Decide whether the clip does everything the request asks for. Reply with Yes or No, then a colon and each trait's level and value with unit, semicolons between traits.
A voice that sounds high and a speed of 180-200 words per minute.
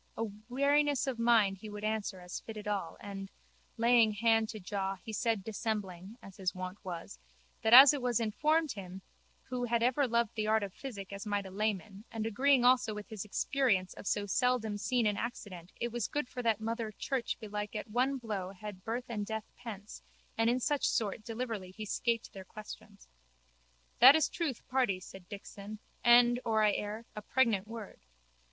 Yes: high, 220 Hz; average, 185 wpm